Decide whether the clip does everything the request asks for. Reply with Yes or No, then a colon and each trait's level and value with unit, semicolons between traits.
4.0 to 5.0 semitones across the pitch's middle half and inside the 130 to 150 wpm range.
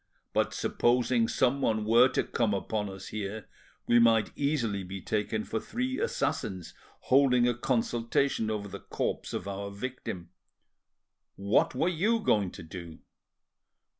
Yes: average, 4.3 semitones; slow, 135 wpm